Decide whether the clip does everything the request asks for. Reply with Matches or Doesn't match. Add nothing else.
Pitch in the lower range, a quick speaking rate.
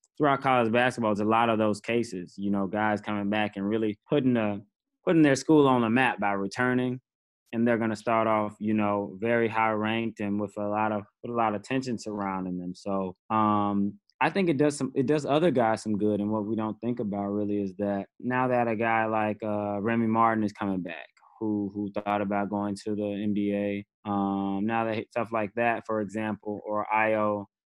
Matches